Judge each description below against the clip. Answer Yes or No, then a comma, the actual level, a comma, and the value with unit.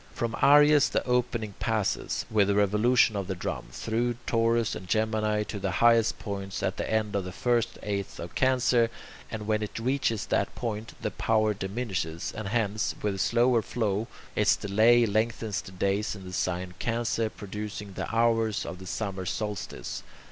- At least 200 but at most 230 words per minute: No, average, 175 wpm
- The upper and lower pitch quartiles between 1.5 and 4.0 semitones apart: Yes, narrow, 2.6 semitones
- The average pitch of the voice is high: No, low, 110 Hz